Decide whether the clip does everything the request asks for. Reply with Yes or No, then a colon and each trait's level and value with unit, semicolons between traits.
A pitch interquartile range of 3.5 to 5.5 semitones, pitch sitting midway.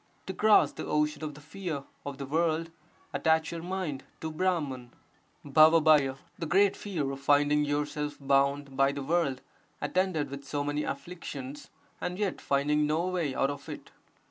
No: average, 3.1 semitones; medium, 150 Hz